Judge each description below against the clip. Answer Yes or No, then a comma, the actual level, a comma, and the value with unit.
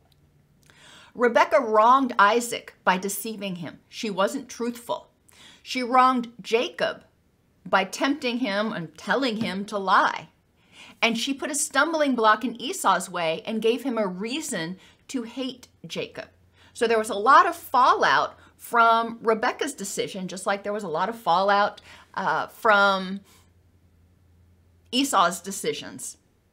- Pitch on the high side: Yes, high, 220 Hz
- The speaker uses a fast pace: No, slow, 135 wpm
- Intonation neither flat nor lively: Yes, average, 4.9 semitones